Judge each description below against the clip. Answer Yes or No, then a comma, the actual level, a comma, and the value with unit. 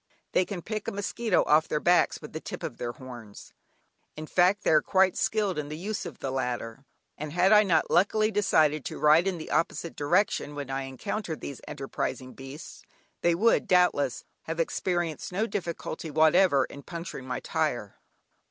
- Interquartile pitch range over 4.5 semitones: Yes, average, 5.0 semitones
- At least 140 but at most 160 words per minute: No, average, 180 wpm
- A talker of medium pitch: Yes, medium, 165 Hz